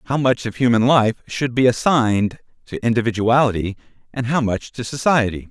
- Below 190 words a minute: Yes, average, 165 wpm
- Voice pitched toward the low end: Yes, low, 120 Hz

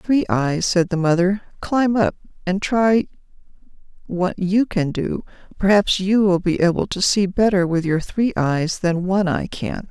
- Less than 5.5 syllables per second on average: Yes, 4.3 syllables/s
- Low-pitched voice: No, high, 190 Hz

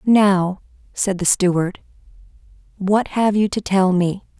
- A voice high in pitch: Yes, high, 195 Hz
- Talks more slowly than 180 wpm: Yes, slow, 135 wpm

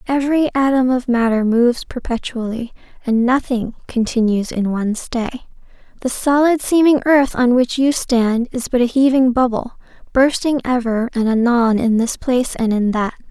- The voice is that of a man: No, female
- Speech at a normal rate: Yes, average, 160 wpm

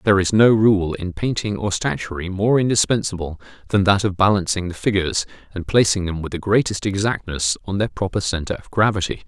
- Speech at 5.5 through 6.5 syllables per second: Yes, 5.8 syllables/s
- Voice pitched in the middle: No, very low, 95 Hz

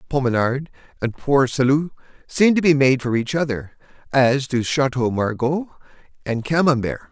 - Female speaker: No, male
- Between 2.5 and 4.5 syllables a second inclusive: Yes, 4.4 syllables/s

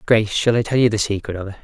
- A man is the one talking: Yes, male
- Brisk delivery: Yes, fast, 330 wpm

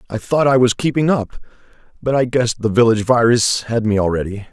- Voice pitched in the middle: No, low, 120 Hz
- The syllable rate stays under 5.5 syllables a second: No, 5.8 syllables/s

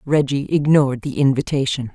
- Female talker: Yes, female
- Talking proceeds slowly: Yes, slow, 125 wpm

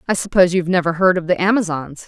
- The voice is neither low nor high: Yes, medium, 180 Hz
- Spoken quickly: Yes, fast, 260 wpm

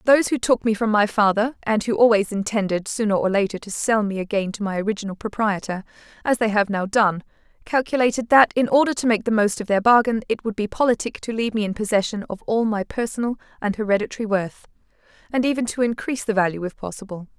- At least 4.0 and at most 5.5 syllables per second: No, 6.3 syllables/s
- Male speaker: No, female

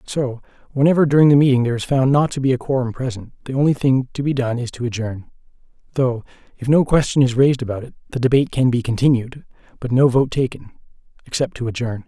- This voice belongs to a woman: No, male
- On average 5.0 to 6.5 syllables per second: No, 6.7 syllables/s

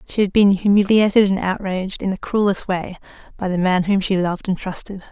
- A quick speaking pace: Yes, fast, 210 wpm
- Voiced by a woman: Yes, female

